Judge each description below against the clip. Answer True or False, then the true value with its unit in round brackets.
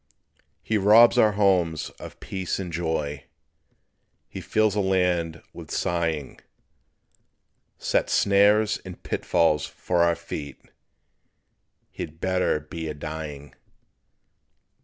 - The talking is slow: True (105 wpm)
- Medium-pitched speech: False (85 Hz)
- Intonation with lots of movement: False (3.9 semitones)